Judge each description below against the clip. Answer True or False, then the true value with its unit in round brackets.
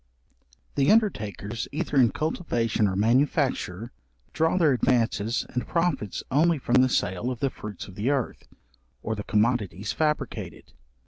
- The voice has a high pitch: False (125 Hz)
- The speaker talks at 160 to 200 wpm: False (140 wpm)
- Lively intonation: True (5.7 semitones)